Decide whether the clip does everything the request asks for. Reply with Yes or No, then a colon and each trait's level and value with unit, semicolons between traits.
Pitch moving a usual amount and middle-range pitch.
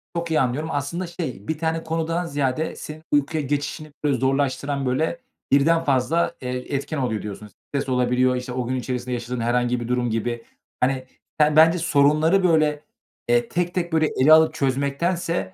Yes: average, 4.2 semitones; medium, 145 Hz